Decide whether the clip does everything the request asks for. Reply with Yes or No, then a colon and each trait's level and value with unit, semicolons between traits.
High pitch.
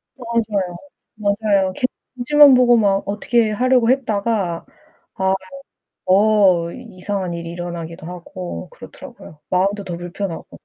Yes: high, 200 Hz